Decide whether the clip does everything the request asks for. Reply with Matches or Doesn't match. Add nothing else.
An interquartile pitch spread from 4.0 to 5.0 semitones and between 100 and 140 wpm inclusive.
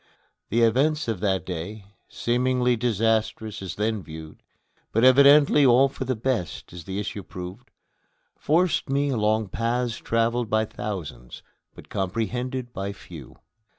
Matches